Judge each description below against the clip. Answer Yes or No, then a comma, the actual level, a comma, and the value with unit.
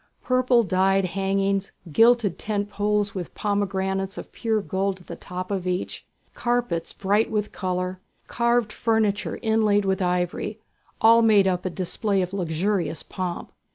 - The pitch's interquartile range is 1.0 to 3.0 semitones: Yes, narrow, 2.5 semitones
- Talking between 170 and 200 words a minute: No, average, 145 wpm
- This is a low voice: No, high, 195 Hz